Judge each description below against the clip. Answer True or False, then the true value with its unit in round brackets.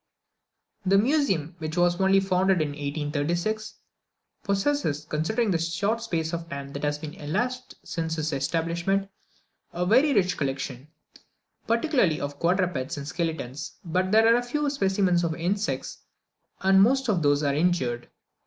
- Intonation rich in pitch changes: False (4.9 semitones)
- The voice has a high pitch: False (175 Hz)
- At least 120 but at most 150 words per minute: True (145 wpm)